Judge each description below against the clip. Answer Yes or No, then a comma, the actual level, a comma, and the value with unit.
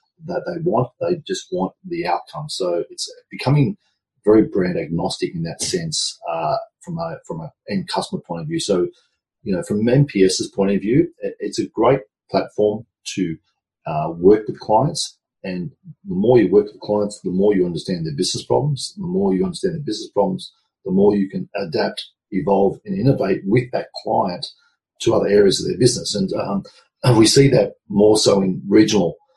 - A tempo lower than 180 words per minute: No, average, 190 wpm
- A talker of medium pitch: Yes, medium, 165 Hz